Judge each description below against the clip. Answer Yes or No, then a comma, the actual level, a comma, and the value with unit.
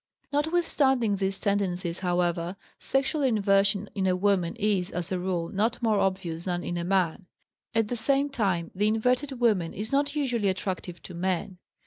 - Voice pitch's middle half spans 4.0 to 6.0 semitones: Yes, average, 4.7 semitones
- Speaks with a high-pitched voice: Yes, high, 195 Hz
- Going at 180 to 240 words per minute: No, average, 165 wpm